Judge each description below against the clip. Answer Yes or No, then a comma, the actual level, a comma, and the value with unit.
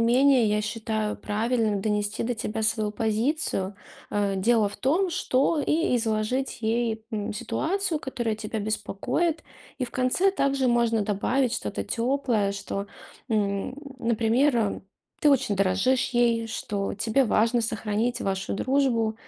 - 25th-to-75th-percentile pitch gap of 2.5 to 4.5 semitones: Yes, average, 3.4 semitones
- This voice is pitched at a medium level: No, high, 225 Hz